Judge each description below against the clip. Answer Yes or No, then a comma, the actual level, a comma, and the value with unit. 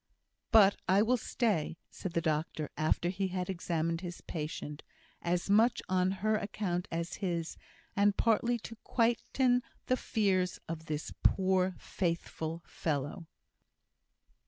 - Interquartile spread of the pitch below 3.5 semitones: No, average, 3.9 semitones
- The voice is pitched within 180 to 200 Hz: Yes, medium, 185 Hz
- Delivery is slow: Yes, slow, 130 wpm